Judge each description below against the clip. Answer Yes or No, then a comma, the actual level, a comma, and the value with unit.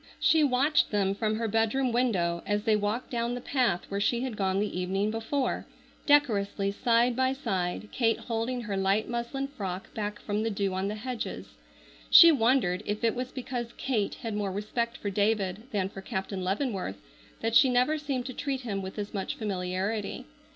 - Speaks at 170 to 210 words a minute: Yes, average, 185 wpm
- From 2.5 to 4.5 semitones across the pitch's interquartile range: Yes, average, 3.9 semitones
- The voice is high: Yes, high, 220 Hz